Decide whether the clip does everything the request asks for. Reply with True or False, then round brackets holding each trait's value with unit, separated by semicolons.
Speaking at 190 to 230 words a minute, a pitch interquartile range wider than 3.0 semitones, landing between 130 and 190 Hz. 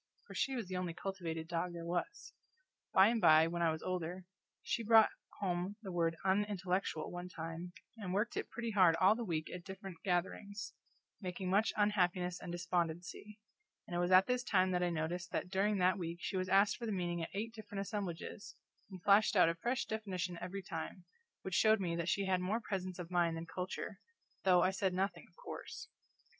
False (200 wpm; 2.6 semitones; 185 Hz)